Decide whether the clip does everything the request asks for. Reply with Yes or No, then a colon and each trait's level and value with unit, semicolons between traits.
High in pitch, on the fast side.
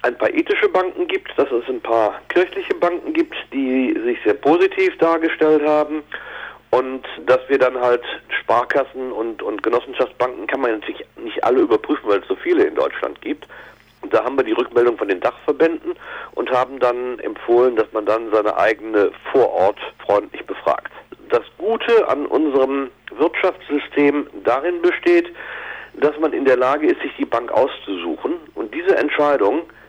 No: very high, 300 Hz; average, 165 wpm